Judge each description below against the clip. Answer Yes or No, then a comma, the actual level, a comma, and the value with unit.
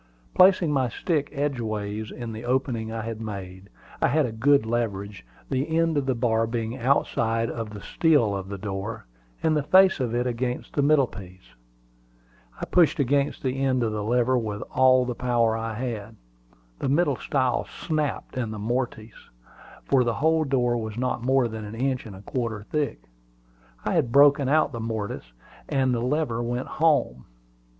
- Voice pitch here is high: No, low, 120 Hz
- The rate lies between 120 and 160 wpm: No, average, 180 wpm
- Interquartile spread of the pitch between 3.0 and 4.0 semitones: Yes, average, 3.7 semitones